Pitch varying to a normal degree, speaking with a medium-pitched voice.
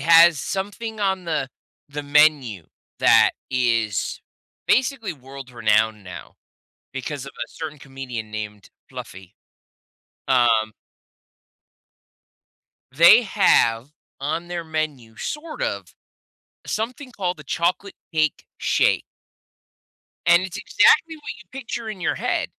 No: wide, 7.9 semitones; medium, 155 Hz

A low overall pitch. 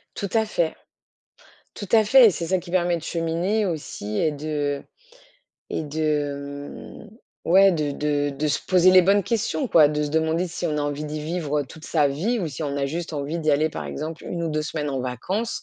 No: medium, 160 Hz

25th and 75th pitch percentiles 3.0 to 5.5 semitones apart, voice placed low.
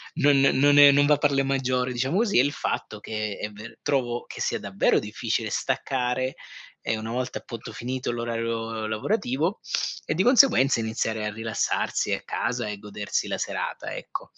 Yes: average, 3.6 semitones; low, 125 Hz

